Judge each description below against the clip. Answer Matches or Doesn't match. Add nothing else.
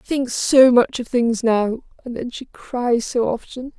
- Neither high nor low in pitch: Doesn't match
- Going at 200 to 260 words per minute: Matches